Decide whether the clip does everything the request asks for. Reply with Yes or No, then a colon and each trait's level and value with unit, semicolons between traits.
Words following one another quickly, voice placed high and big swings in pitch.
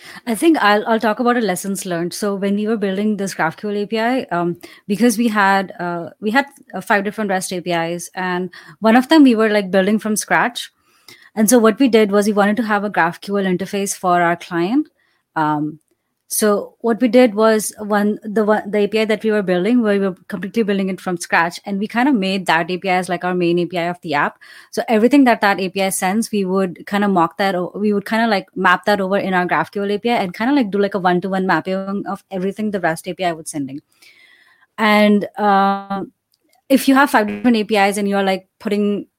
No: fast, 225 wpm; high, 200 Hz; average, 3.1 semitones